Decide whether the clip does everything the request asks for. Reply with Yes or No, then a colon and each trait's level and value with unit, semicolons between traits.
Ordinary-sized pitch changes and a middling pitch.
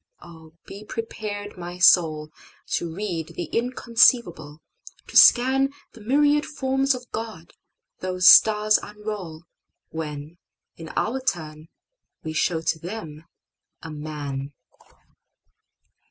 No: wide, 6.1 semitones; medium, 180 Hz